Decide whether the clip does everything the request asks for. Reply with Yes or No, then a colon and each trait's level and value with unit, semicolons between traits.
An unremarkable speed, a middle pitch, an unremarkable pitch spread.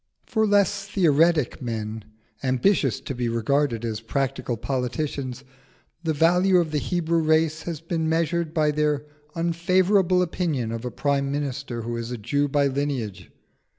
Yes: average, 150 wpm; medium, 145 Hz; average, 5.0 semitones